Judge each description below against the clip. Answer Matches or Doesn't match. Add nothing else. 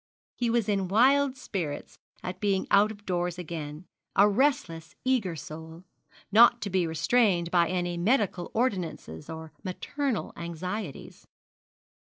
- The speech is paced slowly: Matches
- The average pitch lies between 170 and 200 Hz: Matches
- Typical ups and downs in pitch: Matches